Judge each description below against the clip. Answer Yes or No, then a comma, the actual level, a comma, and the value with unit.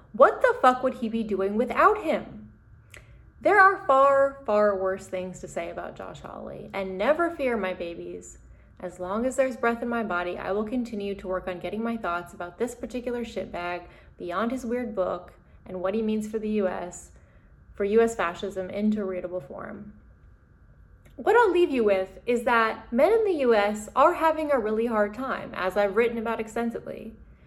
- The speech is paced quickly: No, average, 185 wpm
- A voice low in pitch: No, high, 215 Hz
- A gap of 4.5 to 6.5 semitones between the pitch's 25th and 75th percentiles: Yes, average, 5.0 semitones